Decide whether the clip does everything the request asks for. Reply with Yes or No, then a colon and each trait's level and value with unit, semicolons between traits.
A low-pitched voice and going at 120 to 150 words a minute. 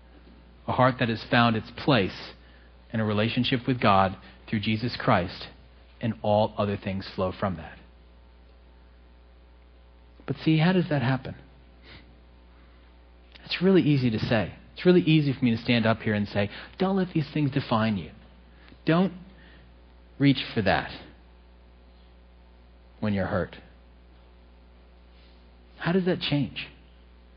Yes: very low, 75 Hz; slow, 135 wpm